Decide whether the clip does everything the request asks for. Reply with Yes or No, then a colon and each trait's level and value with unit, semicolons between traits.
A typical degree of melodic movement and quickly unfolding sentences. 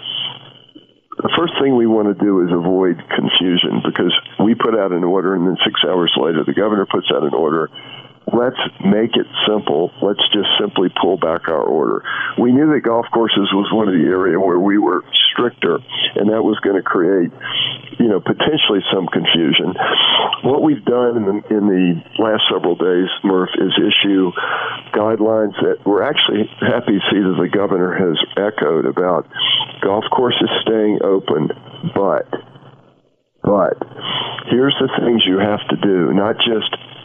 No: average, 3.7 semitones; average, 170 wpm